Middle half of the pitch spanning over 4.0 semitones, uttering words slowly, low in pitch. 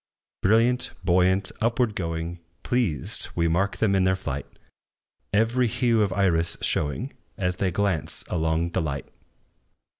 Yes: average, 4.8 semitones; slow, 130 wpm; very low, 95 Hz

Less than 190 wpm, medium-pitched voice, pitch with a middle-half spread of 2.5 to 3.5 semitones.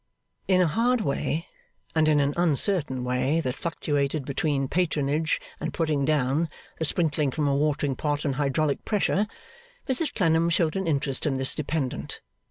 Yes: average, 160 wpm; medium, 150 Hz; average, 3.0 semitones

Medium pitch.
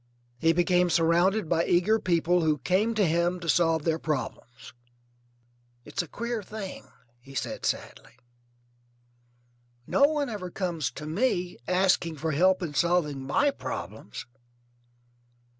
Yes: medium, 175 Hz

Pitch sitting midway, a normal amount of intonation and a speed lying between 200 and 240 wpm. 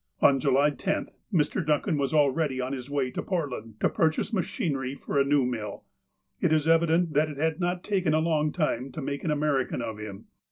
Yes: medium, 145 Hz; average, 3.3 semitones; fast, 205 wpm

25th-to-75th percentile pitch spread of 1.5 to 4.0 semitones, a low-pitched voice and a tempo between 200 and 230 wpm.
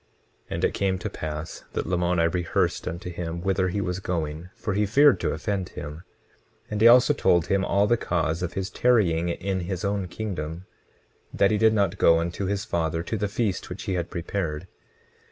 Yes: average, 3.1 semitones; very low, 90 Hz; fast, 205 wpm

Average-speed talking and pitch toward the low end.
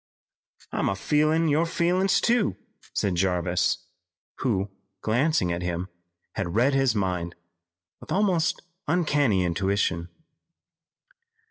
No: slow, 100 wpm; low, 110 Hz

